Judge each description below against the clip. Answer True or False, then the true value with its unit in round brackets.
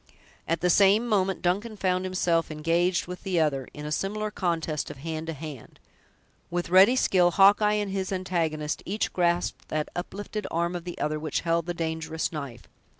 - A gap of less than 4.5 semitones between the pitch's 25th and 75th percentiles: True (3.1 semitones)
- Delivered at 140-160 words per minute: False (180 wpm)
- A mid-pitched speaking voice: True (175 Hz)